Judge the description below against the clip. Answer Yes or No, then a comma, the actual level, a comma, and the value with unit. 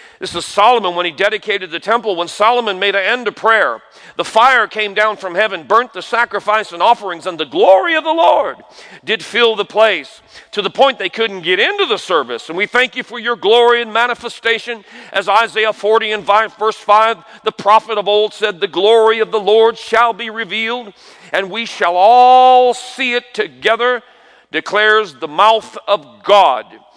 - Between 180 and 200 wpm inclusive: Yes, average, 190 wpm